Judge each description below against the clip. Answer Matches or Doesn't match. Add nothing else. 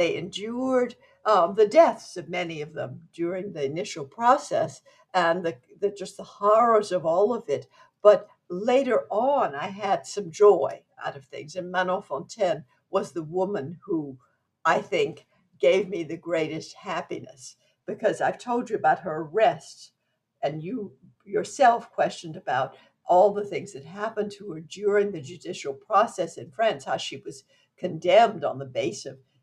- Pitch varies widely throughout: Matches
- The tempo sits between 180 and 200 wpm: Doesn't match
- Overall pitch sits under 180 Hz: Doesn't match